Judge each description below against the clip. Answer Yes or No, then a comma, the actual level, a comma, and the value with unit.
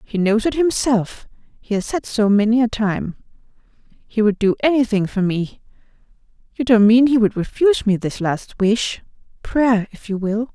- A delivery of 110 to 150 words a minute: No, average, 170 wpm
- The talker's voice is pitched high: Yes, high, 220 Hz